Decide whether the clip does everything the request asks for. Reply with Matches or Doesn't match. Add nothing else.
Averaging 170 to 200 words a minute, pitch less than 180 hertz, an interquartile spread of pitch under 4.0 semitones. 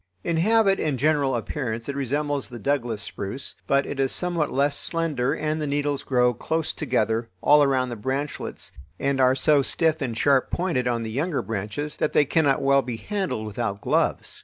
Matches